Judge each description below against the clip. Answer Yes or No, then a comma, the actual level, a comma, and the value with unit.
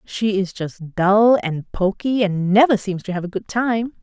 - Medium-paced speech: No, fast, 210 wpm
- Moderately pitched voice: No, high, 205 Hz